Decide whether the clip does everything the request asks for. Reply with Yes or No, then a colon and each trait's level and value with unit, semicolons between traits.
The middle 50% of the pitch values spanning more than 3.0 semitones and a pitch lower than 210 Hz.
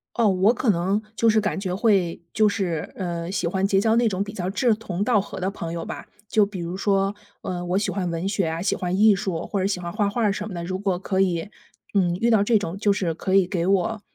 No: average, 2.7 semitones; high, 195 Hz